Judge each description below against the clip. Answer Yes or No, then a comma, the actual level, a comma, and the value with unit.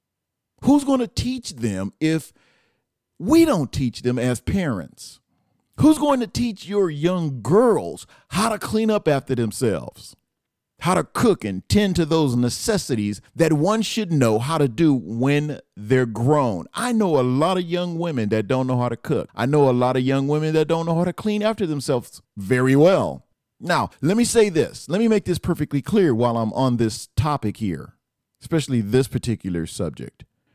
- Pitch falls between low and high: Yes, medium, 145 Hz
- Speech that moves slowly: No, average, 185 wpm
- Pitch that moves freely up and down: Yes, wide, 6.9 semitones